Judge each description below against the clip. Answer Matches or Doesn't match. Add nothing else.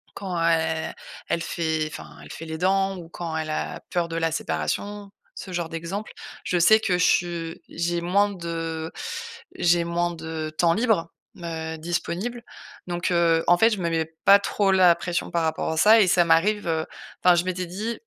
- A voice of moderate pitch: Matches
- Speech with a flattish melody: Matches